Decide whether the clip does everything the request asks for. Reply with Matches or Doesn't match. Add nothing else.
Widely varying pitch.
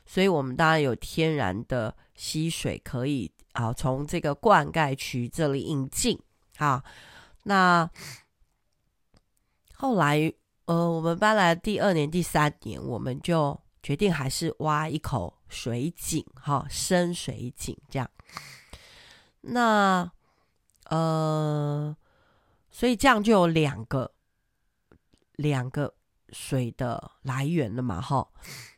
Doesn't match